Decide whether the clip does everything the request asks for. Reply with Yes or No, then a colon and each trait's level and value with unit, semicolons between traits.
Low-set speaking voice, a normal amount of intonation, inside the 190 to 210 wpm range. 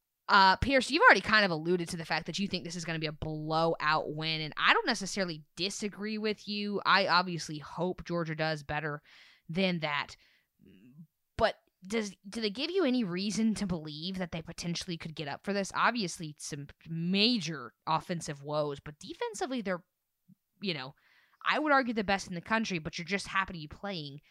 No: medium, 180 Hz; average, 4.0 semitones; average, 195 wpm